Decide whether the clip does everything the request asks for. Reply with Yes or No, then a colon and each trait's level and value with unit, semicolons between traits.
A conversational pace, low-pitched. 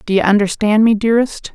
No: average, 195 wpm; high, 215 Hz